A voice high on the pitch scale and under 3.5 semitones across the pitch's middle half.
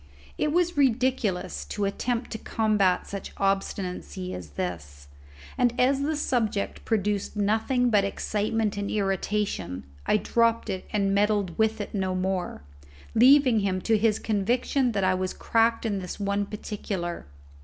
Yes: high, 205 Hz; average, 3.1 semitones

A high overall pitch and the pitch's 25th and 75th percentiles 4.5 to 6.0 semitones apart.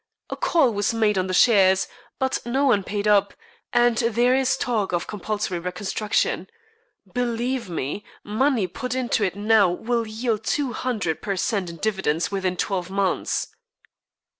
No: high, 210 Hz; average, 4.0 semitones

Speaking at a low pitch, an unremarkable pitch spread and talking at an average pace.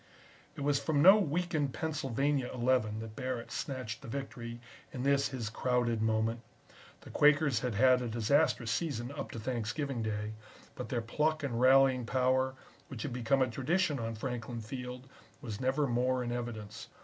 Yes: low, 125 Hz; average, 3.2 semitones; average, 165 wpm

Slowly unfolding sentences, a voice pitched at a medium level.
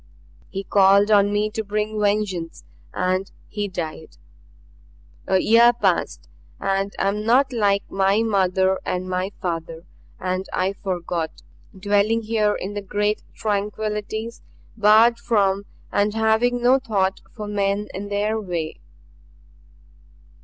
No: slow, 125 wpm; high, 205 Hz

